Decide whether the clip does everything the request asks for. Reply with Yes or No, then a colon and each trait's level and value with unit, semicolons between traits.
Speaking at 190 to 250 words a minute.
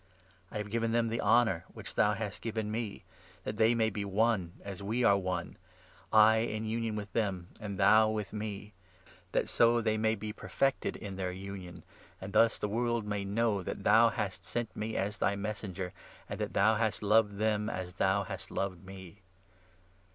Yes: average, 200 wpm